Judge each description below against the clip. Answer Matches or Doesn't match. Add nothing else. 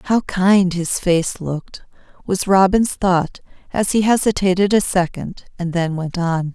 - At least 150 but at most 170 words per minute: Matches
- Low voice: Doesn't match